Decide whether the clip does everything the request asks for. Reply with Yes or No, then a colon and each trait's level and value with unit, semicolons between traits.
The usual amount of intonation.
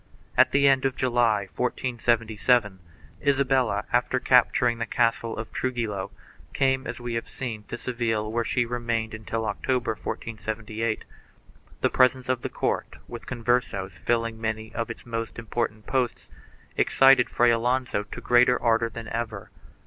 No: narrow, 1.9 semitones